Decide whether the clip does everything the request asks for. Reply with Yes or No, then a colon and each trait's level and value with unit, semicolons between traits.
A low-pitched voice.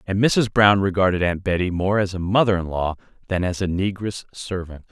Yes: very low, 95 Hz